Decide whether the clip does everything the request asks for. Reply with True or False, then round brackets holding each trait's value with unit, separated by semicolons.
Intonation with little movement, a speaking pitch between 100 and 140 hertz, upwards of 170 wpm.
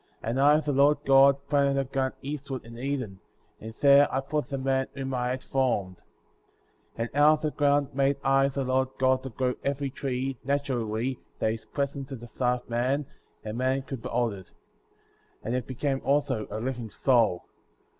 True (2.2 semitones; 135 Hz; 195 wpm)